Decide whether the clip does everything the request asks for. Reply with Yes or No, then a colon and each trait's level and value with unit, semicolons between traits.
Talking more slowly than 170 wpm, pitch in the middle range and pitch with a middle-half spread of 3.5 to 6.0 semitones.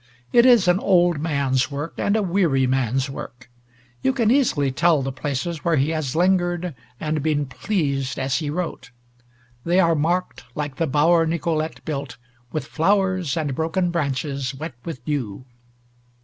Yes: average, 160 wpm; medium, 155 Hz; average, 4.3 semitones